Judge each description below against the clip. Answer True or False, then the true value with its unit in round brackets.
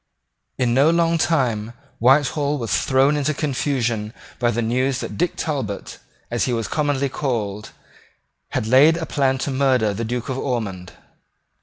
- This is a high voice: False (130 Hz)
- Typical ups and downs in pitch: True (3.8 semitones)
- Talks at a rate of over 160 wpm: False (155 wpm)